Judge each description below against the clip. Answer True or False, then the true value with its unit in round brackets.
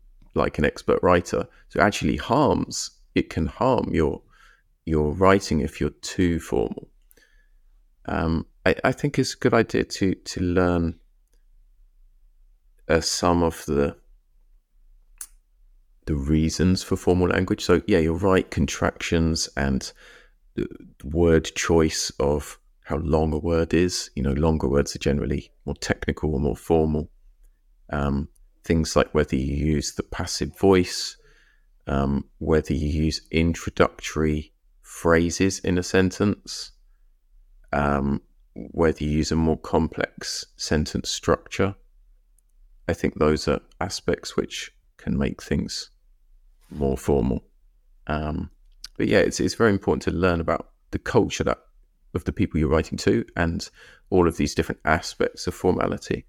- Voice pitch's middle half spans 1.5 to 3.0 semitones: False (3.6 semitones)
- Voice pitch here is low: True (80 Hz)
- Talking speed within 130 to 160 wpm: True (135 wpm)